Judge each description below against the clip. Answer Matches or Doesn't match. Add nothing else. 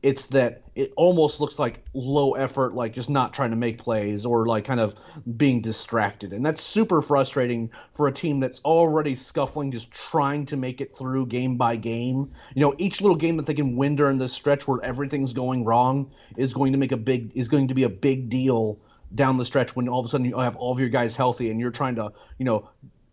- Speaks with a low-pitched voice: Matches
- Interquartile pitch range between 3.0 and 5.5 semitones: Doesn't match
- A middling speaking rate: Doesn't match